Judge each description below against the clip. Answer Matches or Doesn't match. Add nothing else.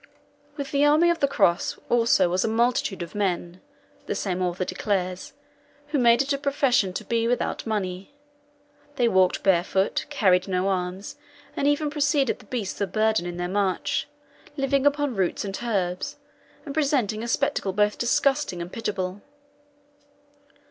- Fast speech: Doesn't match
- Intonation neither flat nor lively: Doesn't match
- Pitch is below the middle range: Doesn't match